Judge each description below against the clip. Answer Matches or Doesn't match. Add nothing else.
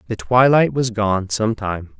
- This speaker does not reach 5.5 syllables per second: Matches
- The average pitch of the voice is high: Doesn't match